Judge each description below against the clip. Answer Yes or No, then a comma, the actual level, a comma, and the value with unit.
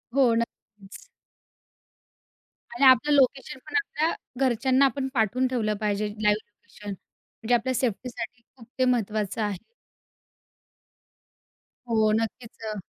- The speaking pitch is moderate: No, high, 230 Hz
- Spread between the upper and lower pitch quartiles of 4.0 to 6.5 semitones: No, average, 3.5 semitones